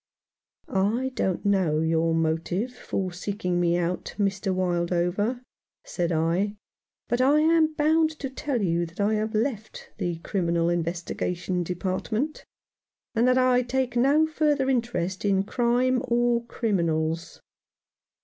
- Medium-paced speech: No, slow, 130 wpm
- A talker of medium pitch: No, high, 200 Hz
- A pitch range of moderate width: No, wide, 6.2 semitones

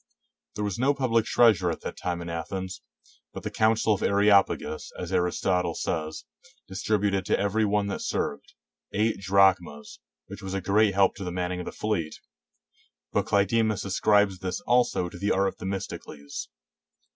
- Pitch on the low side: Yes, very low, 95 Hz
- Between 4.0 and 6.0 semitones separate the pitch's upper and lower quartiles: No, average, 2.7 semitones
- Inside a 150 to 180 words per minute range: Yes, average, 170 wpm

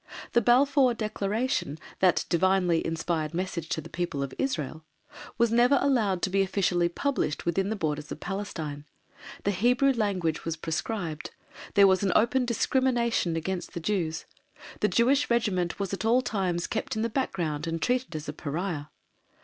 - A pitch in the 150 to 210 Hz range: Yes, high, 190 Hz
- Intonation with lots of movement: Yes, wide, 6.1 semitones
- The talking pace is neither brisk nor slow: Yes, average, 160 wpm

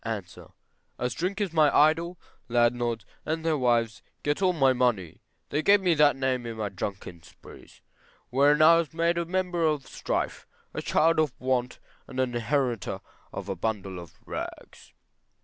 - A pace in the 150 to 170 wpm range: Yes, average, 165 wpm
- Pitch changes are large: Yes, wide, 5.7 semitones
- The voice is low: Yes, low, 130 Hz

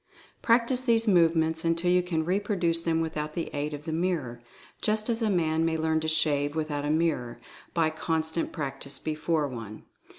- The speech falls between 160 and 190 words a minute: Yes, average, 175 wpm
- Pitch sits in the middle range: Yes, medium, 160 Hz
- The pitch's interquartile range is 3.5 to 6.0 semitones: No, narrow, 2.5 semitones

